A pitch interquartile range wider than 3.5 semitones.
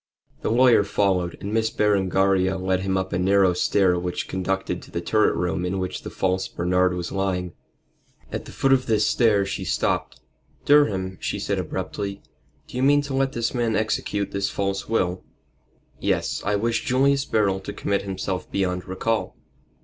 No: average, 3.0 semitones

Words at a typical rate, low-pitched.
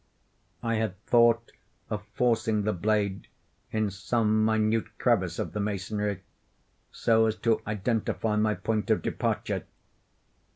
No: slow, 125 wpm; low, 110 Hz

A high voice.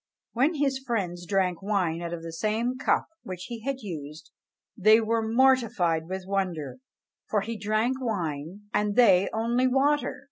Yes: high, 210 Hz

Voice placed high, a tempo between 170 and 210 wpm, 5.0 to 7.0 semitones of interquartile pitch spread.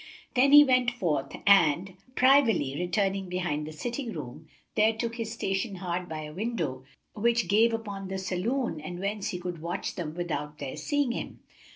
Yes: high, 195 Hz; average, 175 wpm; wide, 5.4 semitones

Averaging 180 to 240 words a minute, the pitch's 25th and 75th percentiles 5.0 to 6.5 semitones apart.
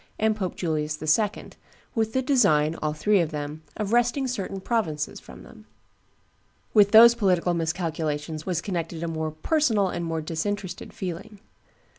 No: average, 150 wpm; average, 5.3 semitones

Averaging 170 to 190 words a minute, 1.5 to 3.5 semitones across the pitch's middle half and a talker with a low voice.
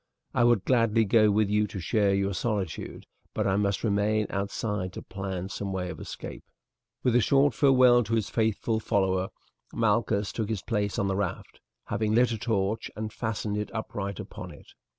Yes: average, 185 wpm; narrow, 2.4 semitones; low, 105 Hz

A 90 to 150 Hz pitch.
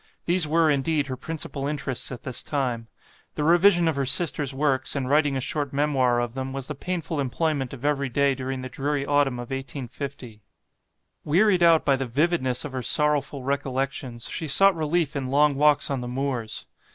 Yes: medium, 140 Hz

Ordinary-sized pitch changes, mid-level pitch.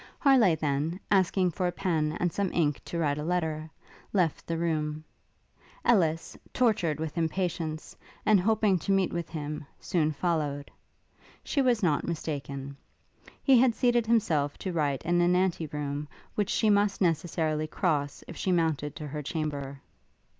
Yes: average, 3.8 semitones; medium, 165 Hz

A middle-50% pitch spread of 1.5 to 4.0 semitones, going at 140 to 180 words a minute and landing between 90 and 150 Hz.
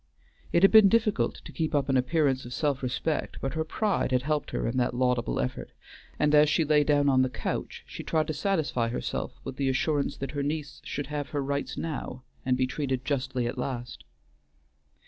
No: average, 3.0 semitones; fast, 205 wpm; medium, 140 Hz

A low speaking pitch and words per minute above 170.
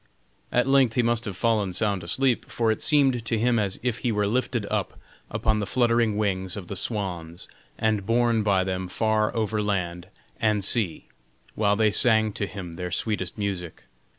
Yes: low, 105 Hz; average, 180 wpm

